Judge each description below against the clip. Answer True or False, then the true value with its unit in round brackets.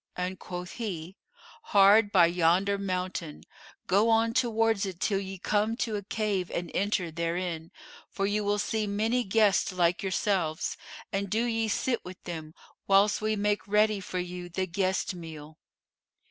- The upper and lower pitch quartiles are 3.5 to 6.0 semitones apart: False (2.9 semitones)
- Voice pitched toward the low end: False (195 Hz)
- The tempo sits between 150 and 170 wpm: True (160 wpm)